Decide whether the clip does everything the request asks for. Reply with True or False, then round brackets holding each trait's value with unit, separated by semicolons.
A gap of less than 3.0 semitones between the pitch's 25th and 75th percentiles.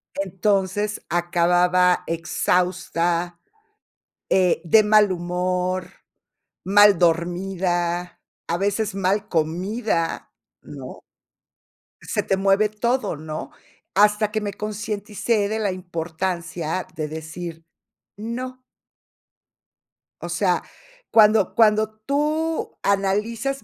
False (3.3 semitones)